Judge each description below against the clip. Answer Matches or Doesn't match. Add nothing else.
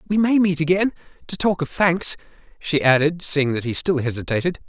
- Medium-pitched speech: Matches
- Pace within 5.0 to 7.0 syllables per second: Matches